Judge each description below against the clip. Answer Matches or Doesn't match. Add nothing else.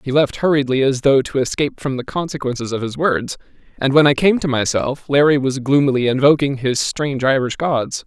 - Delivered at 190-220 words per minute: Matches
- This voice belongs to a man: Matches